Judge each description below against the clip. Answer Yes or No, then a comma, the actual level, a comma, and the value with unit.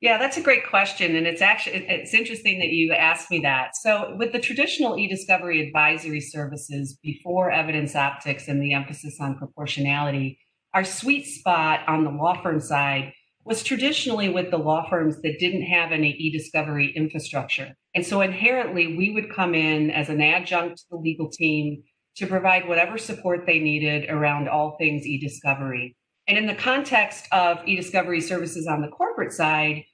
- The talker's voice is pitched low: No, medium, 165 Hz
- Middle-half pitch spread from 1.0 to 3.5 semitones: No, average, 4.1 semitones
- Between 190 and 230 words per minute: No, average, 170 wpm